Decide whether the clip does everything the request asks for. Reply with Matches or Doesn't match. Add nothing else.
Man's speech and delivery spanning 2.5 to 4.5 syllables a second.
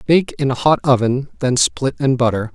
Doesn't match